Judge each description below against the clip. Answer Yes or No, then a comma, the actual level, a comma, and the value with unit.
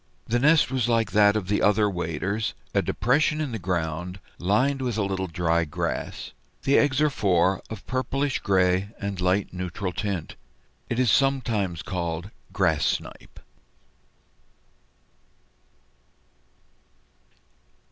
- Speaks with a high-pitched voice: No, low, 100 Hz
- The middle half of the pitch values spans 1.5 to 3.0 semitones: No, average, 5.1 semitones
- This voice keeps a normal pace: No, slow, 125 wpm